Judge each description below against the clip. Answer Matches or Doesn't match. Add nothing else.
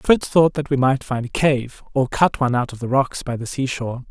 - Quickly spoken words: Matches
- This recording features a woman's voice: Doesn't match